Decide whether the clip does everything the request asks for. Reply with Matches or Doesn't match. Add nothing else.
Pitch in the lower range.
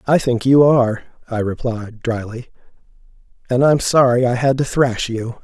Matches